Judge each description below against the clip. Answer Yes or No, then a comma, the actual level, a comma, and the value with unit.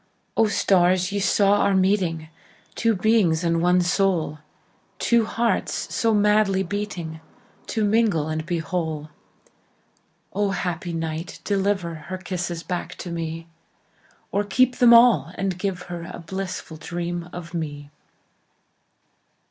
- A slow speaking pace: Yes, slow, 110 wpm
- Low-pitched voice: No, medium, 180 Hz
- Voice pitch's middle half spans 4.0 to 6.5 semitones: No, average, 3.5 semitones